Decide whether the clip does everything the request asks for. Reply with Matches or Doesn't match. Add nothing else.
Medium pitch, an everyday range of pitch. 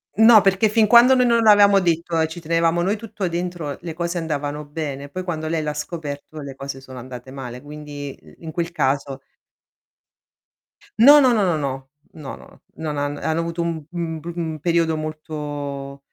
Matches